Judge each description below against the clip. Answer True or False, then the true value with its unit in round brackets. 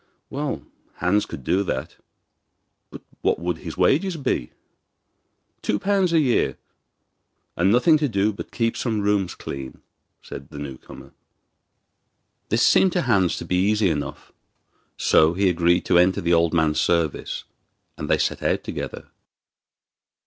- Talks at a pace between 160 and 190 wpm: False (150 wpm)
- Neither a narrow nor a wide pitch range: False (5.8 semitones)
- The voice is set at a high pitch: False (95 Hz)